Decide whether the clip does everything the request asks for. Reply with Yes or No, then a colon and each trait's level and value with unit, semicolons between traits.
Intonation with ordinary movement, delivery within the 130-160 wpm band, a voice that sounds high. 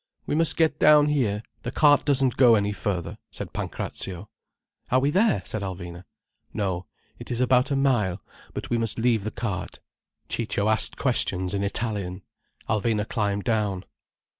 No: average, 4.5 semitones; average, 155 wpm; low, 110 Hz